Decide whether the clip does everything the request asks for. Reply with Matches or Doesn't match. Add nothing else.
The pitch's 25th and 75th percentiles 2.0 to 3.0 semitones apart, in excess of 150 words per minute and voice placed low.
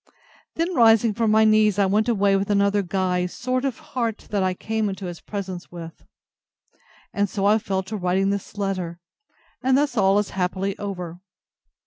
Doesn't match